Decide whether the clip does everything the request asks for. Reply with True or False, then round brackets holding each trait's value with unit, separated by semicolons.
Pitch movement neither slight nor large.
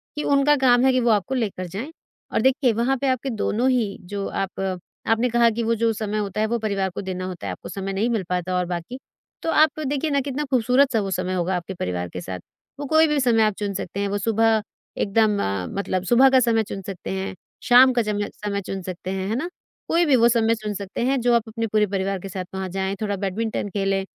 True (4.1 semitones)